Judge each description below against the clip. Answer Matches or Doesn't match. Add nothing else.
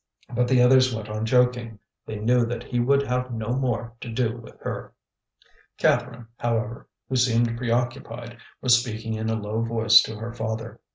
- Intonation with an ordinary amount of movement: Doesn't match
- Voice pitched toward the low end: Matches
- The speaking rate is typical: Matches